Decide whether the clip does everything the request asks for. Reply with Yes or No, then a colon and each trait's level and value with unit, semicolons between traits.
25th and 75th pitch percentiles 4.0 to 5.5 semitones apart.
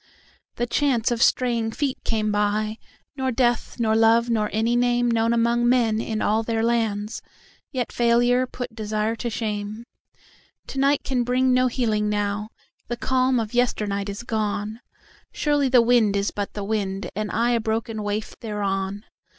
No: narrow, 2.4 semitones